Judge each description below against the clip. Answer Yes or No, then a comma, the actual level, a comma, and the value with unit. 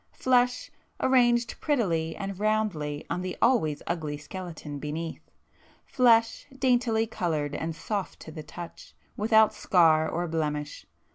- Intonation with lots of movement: Yes, wide, 6.3 semitones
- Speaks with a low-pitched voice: No, medium, 180 Hz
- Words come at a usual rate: No, slow, 120 wpm